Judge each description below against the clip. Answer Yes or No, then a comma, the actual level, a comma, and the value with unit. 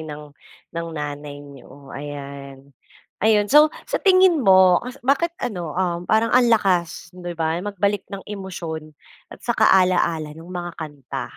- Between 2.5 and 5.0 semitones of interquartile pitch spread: No, wide, 5.5 semitones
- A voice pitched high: No, medium, 175 Hz